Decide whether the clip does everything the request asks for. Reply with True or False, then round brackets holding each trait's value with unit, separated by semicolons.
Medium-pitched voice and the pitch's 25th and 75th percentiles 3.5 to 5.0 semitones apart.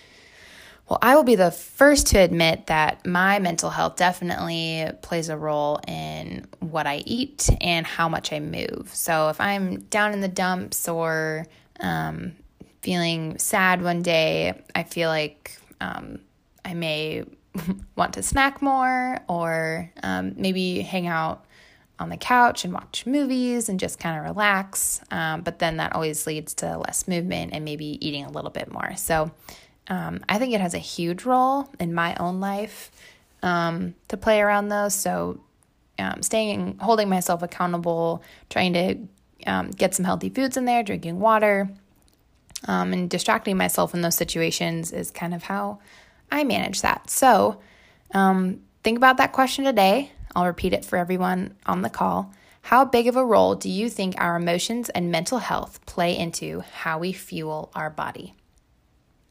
True (175 Hz; 4.0 semitones)